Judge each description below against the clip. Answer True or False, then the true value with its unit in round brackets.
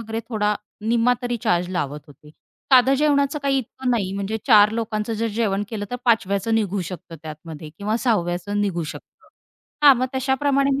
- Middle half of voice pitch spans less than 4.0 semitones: False (4.3 semitones)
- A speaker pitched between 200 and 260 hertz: True (220 Hz)